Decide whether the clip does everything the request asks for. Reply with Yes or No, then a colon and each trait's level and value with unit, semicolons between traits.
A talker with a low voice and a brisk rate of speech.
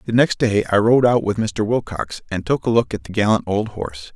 Yes: low, 110 Hz; fast, 260 wpm